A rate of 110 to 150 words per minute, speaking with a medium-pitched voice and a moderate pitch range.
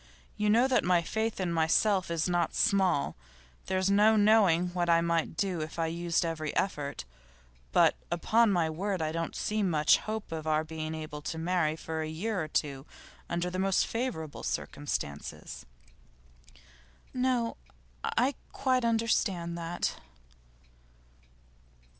Yes: average, 140 wpm; medium, 175 Hz; average, 4.6 semitones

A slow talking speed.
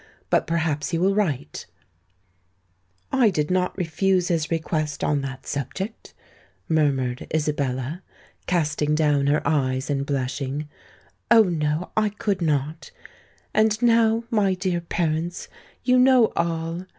Yes: slow, 120 wpm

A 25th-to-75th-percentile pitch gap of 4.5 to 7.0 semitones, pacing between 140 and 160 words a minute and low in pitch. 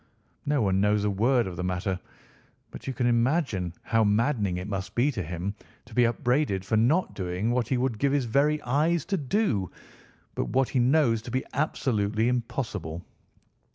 No: average, 5.2 semitones; average, 185 wpm; low, 115 Hz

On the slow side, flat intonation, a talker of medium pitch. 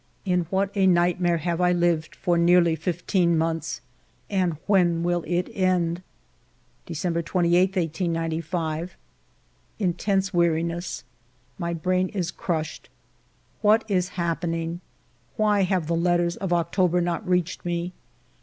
Yes: slow, 120 wpm; narrow, 1.5 semitones; medium, 175 Hz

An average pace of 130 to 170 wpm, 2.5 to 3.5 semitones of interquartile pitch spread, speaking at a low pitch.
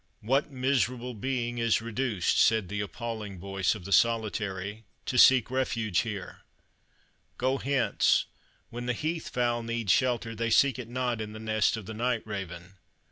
Yes: average, 160 wpm; average, 3.0 semitones; low, 115 Hz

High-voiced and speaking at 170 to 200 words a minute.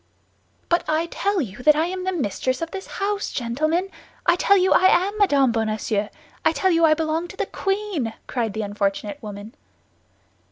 Yes: very high, 315 Hz; average, 185 wpm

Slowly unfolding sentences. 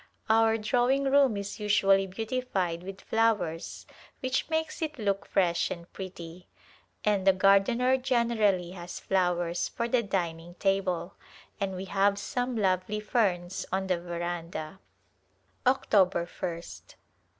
Yes: slow, 125 wpm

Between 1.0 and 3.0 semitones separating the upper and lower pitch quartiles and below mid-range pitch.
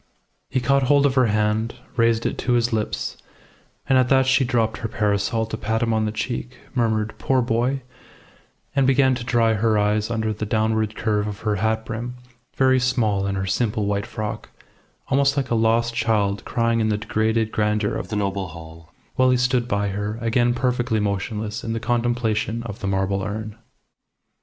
Yes: narrow, 2.4 semitones; low, 110 Hz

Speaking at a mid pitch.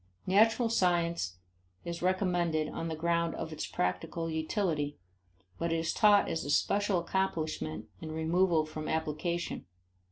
Yes: medium, 165 Hz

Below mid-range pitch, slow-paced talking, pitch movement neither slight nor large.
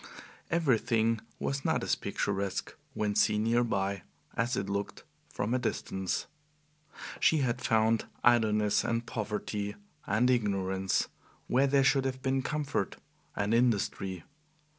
Yes: low, 110 Hz; slow, 125 wpm; average, 3.8 semitones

